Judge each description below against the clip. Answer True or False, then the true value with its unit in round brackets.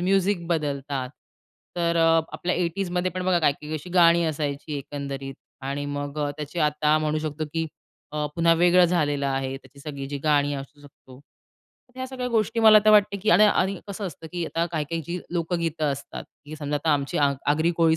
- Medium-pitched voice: True (160 Hz)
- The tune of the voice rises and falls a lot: False (3.6 semitones)